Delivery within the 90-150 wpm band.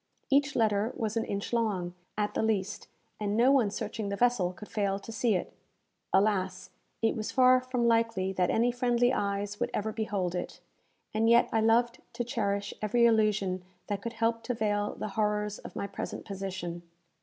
No: average, 185 wpm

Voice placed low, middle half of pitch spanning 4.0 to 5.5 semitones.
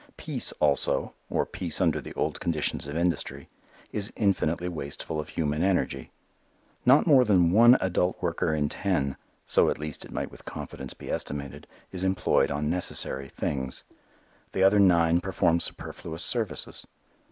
Yes: very low, 85 Hz; average, 4.3 semitones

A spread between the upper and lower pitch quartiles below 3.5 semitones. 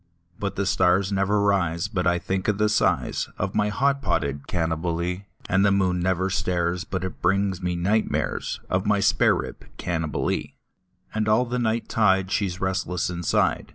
Yes: narrow, 2.5 semitones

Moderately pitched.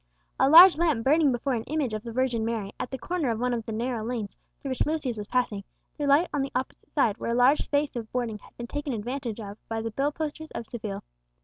No: very high, 250 Hz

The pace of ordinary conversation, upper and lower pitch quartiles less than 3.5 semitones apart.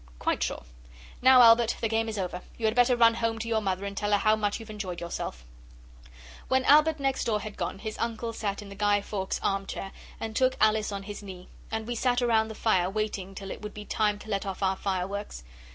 No: fast, 230 wpm; narrow, 2.5 semitones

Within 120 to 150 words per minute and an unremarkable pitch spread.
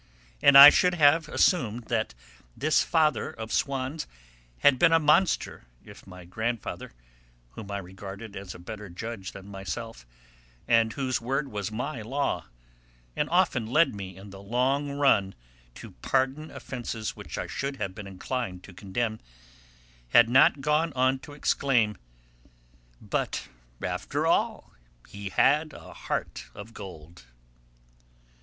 No: average, 140 wpm; wide, 5.8 semitones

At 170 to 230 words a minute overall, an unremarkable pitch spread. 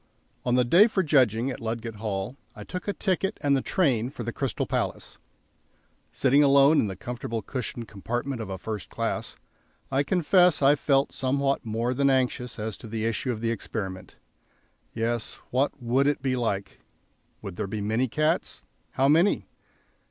Yes: average, 175 wpm; average, 3.9 semitones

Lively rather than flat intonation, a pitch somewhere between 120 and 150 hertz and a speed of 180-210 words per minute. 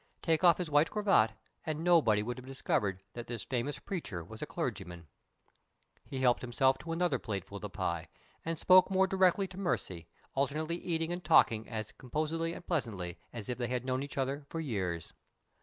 Yes: wide, 7.0 semitones; low, 135 Hz; average, 190 wpm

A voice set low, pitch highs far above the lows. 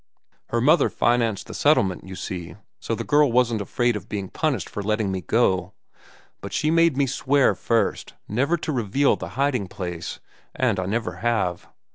Yes: low, 115 Hz; wide, 5.8 semitones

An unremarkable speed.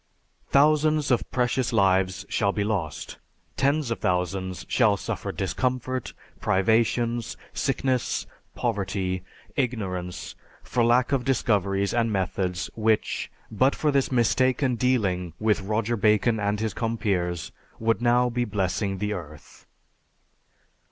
No: slow, 120 wpm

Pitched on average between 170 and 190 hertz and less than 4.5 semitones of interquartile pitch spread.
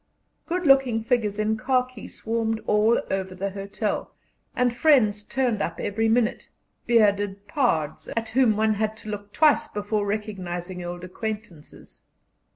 No: high, 215 Hz; average, 2.9 semitones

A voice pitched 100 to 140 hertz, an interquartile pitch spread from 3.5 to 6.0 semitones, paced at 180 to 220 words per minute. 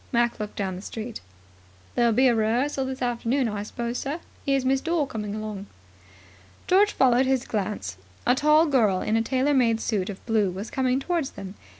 No: high, 240 Hz; average, 3.9 semitones; average, 190 wpm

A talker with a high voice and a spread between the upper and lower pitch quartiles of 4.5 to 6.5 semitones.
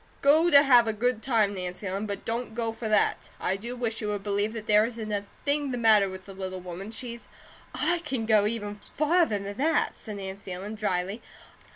No: high, 215 Hz; average, 3.3 semitones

